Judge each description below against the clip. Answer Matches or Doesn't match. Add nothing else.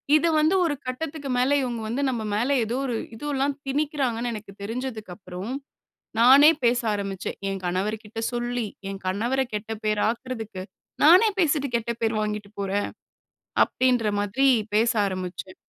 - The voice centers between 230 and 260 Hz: Matches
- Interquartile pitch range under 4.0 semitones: Doesn't match